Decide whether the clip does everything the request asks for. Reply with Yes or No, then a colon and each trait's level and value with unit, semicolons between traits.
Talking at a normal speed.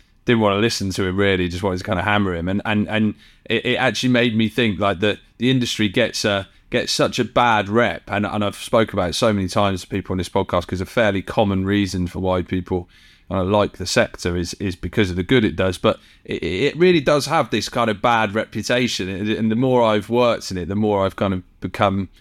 No: fast, 250 wpm